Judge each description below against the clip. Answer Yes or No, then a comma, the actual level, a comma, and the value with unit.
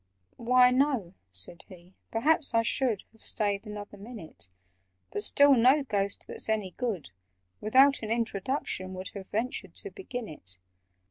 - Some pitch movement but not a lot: Yes, average, 4.8 semitones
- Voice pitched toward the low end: No, high, 220 Hz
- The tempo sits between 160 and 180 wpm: No, average, 145 wpm